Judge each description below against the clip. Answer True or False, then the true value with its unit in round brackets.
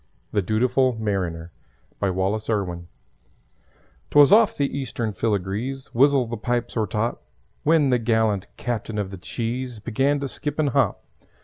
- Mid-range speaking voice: False (115 Hz)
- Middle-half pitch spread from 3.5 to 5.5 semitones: True (4.5 semitones)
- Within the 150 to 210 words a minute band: False (140 wpm)